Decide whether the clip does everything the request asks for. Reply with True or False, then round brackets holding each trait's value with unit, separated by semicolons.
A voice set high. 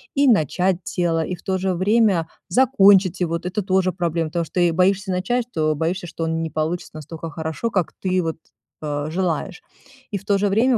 False (180 Hz)